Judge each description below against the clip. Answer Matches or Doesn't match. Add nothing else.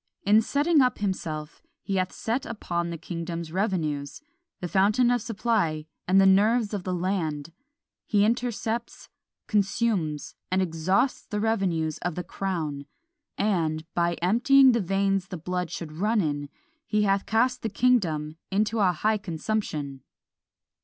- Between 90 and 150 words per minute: Matches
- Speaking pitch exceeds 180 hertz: Matches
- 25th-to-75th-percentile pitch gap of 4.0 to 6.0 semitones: Matches